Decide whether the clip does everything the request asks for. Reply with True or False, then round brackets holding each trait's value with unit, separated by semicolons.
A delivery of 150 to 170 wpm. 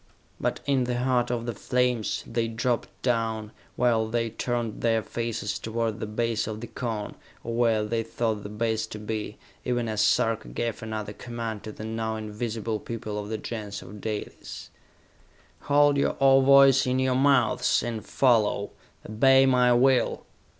True (165 wpm)